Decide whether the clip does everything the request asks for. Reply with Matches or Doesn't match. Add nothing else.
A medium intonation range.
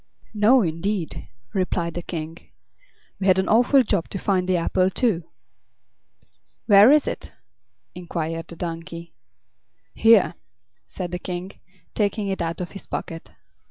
Matches